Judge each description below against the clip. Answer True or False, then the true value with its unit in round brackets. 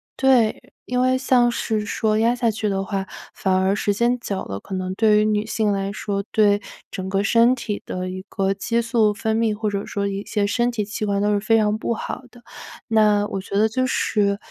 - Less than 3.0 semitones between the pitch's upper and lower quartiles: True (2.4 semitones)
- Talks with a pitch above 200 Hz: True (210 Hz)